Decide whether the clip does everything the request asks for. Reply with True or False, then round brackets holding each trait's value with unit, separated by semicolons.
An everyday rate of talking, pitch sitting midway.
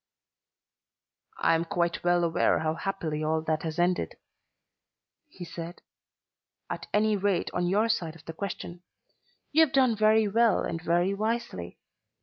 True (145 wpm; 175 Hz)